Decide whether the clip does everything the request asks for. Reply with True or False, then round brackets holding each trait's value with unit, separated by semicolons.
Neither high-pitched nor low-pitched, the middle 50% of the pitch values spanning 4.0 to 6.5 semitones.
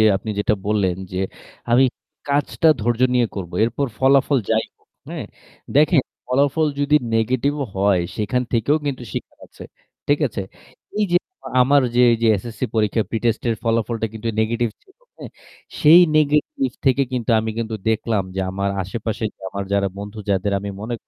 False (115 Hz; 4.6 semitones)